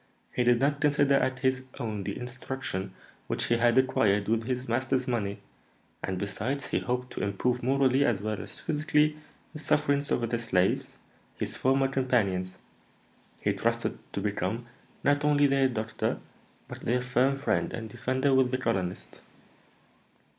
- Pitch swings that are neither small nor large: Yes, average, 3.8 semitones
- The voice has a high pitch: No, low, 125 Hz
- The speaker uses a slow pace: No, average, 155 wpm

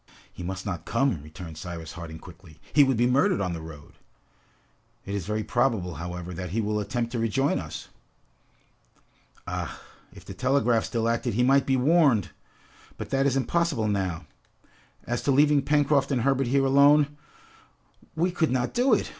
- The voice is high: No, low, 120 Hz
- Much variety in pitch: Yes, wide, 7.1 semitones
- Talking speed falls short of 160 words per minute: No, average, 170 wpm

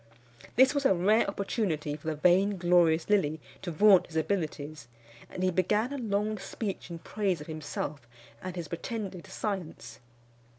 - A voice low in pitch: No, medium, 180 Hz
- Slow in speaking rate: No, average, 155 wpm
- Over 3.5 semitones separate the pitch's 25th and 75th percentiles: Yes, average, 4.5 semitones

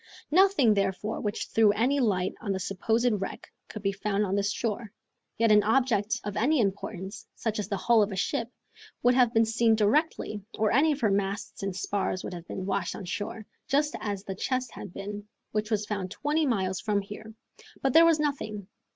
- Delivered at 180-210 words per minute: Yes, fast, 205 wpm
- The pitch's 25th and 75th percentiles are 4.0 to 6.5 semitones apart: No, average, 3.1 semitones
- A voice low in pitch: No, high, 210 Hz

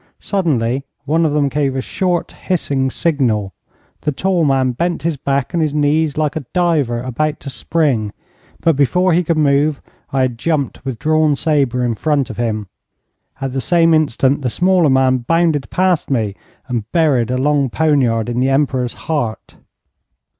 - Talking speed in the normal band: Yes, average, 170 wpm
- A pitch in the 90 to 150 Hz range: Yes, medium, 140 Hz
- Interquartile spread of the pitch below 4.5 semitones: Yes, average, 3.8 semitones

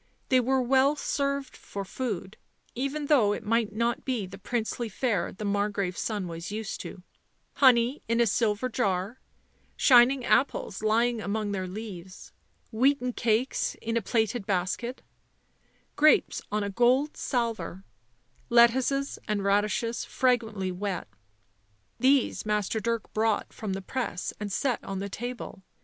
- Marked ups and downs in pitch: No, average, 3.7 semitones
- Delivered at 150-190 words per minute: No, average, 140 wpm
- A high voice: Yes, high, 225 Hz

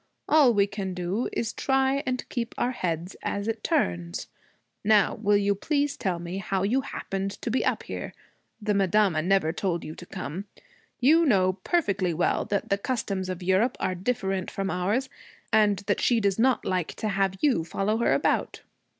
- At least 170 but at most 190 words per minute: Yes, average, 185 wpm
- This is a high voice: Yes, high, 200 Hz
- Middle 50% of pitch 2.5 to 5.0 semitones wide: Yes, average, 3.9 semitones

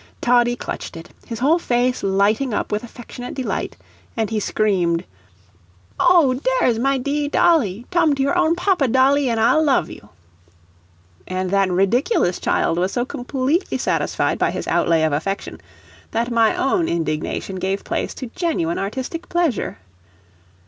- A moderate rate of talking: Yes, average, 155 wpm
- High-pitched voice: Yes, high, 245 Hz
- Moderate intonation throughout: No, wide, 6.3 semitones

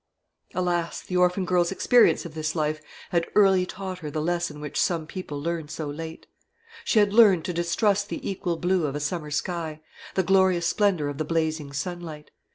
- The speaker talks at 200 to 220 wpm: No, average, 185 wpm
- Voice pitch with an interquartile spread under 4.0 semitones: Yes, average, 3.1 semitones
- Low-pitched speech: No, medium, 170 Hz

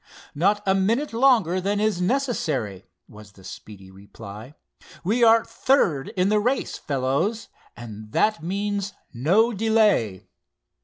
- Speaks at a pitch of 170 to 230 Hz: Yes, high, 190 Hz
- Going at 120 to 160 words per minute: Yes, slow, 135 wpm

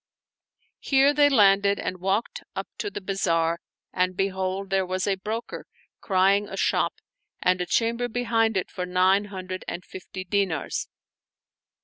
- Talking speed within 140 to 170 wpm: Yes, average, 145 wpm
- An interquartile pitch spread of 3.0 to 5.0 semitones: No, narrow, 2.5 semitones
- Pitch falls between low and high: No, high, 195 Hz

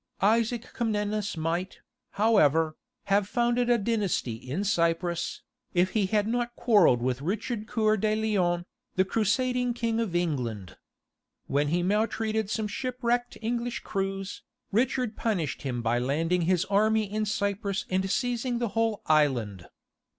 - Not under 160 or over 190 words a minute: No, slow, 135 wpm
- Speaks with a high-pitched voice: Yes, high, 205 Hz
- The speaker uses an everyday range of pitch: Yes, average, 4.9 semitones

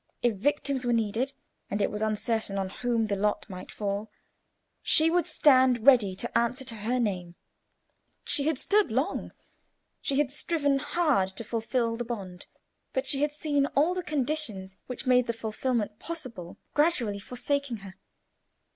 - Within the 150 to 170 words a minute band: Yes, average, 160 wpm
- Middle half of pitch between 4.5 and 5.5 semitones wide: Yes, average, 5.2 semitones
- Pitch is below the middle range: No, high, 245 Hz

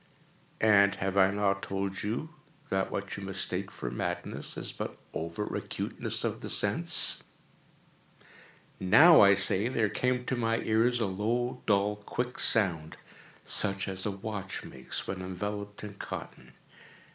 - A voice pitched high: No, low, 100 Hz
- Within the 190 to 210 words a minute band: No, average, 140 wpm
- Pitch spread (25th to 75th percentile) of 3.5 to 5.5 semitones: No, narrow, 2.5 semitones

